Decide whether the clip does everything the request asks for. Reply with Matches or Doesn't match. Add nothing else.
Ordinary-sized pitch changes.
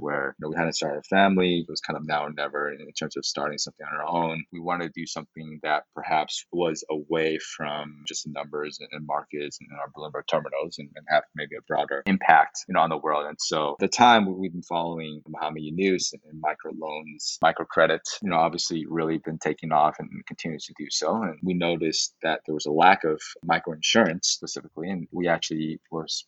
Doesn't match